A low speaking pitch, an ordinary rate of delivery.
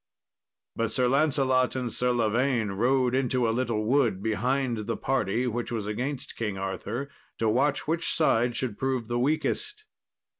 Yes: low, 125 Hz; average, 155 wpm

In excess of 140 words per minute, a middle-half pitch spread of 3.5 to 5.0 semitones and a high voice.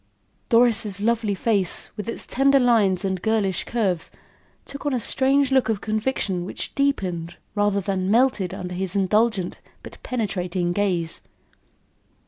No: slow, 135 wpm; average, 4.1 semitones; high, 205 Hz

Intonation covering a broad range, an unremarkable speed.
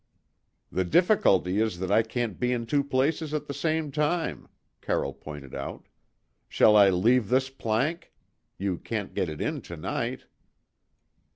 Yes: wide, 6.9 semitones; average, 155 wpm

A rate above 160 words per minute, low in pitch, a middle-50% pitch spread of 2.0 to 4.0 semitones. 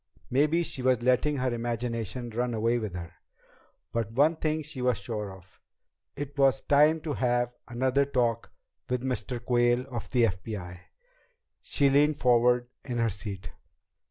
No: average, 155 wpm; low, 120 Hz; average, 2.7 semitones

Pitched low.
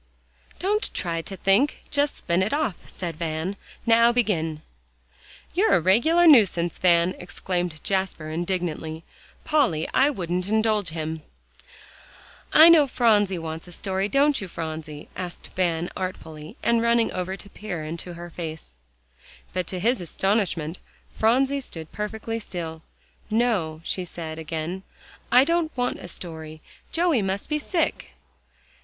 No: medium, 185 Hz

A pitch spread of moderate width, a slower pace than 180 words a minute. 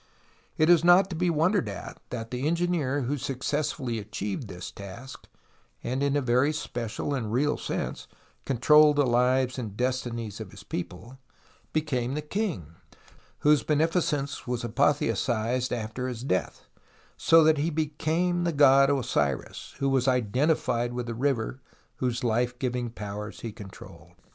Yes: average, 4.1 semitones; average, 150 wpm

